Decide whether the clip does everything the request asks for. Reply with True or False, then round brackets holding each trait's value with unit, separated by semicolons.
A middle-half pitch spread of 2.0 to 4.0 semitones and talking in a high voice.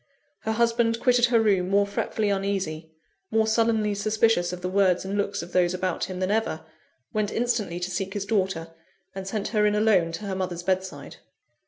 True (3.1 semitones; 200 Hz)